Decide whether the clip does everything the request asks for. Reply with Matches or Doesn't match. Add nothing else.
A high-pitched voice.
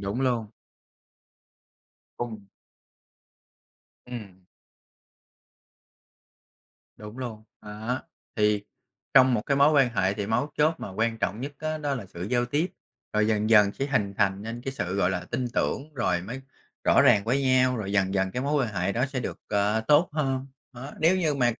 Doesn't match